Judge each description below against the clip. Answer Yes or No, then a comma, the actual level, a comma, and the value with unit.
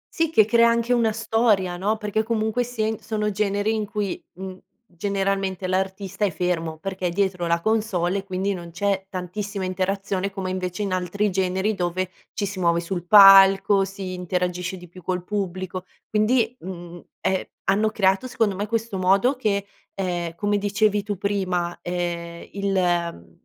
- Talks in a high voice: Yes, high, 195 Hz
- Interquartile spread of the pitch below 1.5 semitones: No, narrow, 2.5 semitones